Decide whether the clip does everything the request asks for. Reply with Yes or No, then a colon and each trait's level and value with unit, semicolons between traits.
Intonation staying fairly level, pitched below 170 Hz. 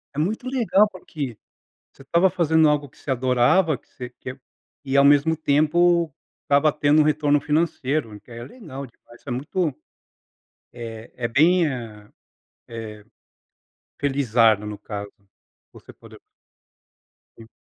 No: average, 5.1 semitones; medium, 140 Hz